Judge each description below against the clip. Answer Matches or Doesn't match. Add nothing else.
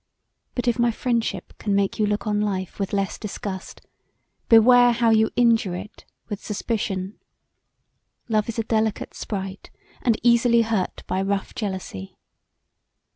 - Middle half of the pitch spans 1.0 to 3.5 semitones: Matches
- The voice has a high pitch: Matches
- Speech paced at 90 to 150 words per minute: Matches